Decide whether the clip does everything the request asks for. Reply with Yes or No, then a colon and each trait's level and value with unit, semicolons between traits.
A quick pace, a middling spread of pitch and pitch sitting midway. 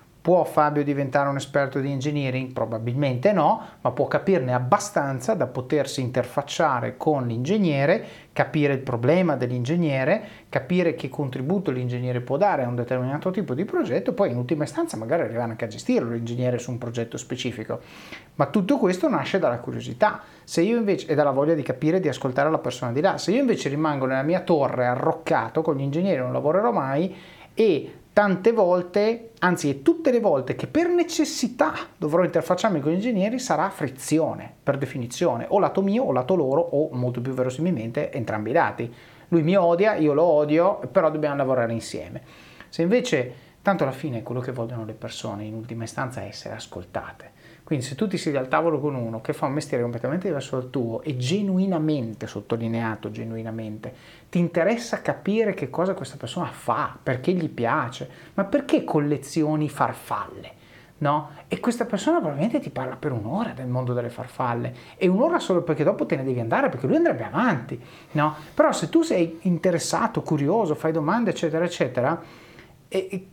No: fast, 175 wpm; wide, 6.2 semitones; medium, 150 Hz